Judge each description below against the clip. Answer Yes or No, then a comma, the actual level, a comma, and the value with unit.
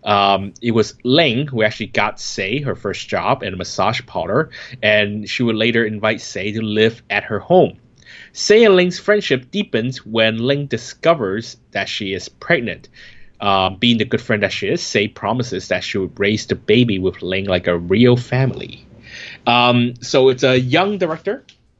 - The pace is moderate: Yes, average, 180 wpm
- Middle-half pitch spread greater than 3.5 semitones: Yes, average, 3.9 semitones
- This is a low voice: Yes, low, 120 Hz